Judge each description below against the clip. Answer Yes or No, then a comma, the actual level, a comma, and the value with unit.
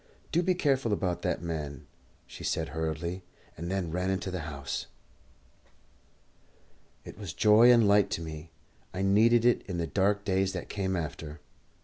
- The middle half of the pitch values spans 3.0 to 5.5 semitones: Yes, average, 4.1 semitones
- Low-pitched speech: Yes, very low, 95 Hz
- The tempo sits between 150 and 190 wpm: Yes, average, 165 wpm